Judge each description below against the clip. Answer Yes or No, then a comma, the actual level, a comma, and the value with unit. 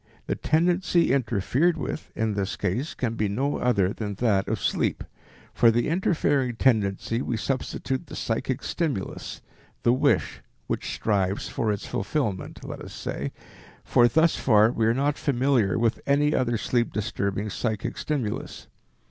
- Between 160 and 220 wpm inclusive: No, average, 150 wpm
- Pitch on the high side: No, low, 120 Hz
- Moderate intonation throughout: Yes, average, 5.0 semitones